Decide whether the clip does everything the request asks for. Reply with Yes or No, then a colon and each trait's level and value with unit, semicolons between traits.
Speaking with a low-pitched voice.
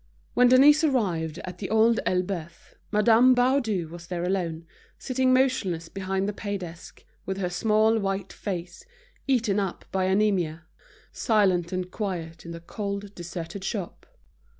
No: high, 195 Hz